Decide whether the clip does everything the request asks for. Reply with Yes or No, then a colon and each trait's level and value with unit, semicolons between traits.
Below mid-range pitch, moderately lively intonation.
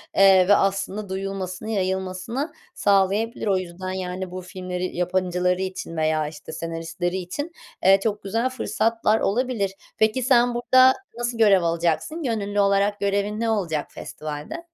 No: high, 195 Hz; average, 3.3 semitones